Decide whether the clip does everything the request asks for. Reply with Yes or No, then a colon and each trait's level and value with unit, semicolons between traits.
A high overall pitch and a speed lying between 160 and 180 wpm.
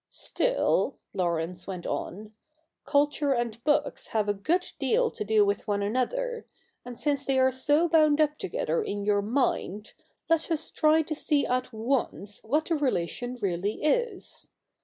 Yes: very high, 260 Hz; average, 165 wpm